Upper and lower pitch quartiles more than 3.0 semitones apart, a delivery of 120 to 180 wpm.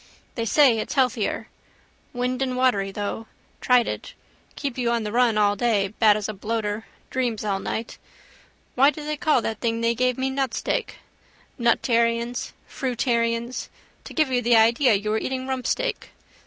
No: average, 2.7 semitones; average, 155 wpm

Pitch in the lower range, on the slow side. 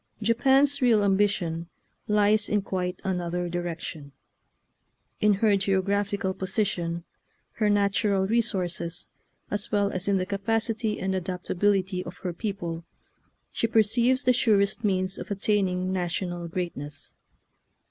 No: high, 195 Hz; slow, 125 wpm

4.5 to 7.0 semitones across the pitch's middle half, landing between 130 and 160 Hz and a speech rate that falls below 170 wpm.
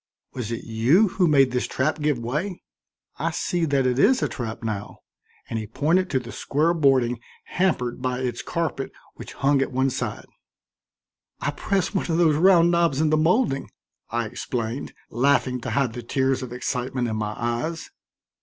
No: average, 5.0 semitones; low, 135 Hz; average, 180 wpm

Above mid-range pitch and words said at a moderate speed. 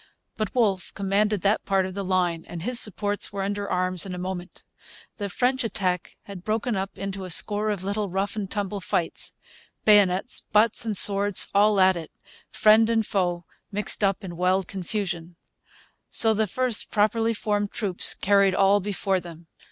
Yes: high, 200 Hz; average, 175 wpm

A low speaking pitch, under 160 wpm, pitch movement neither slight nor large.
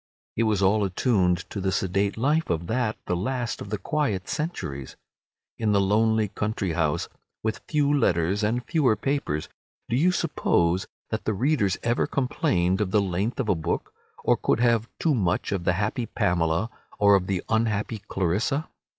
No: low, 105 Hz; average, 175 wpm; average, 4.3 semitones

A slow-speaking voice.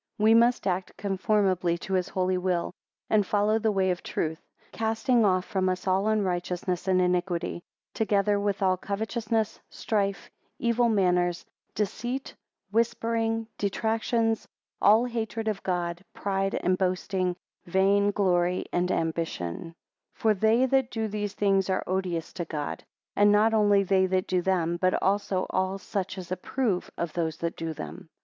No: average, 155 wpm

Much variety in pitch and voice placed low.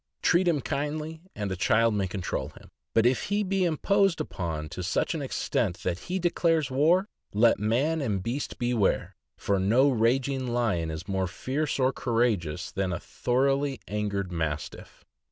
Yes: wide, 7.1 semitones; low, 120 Hz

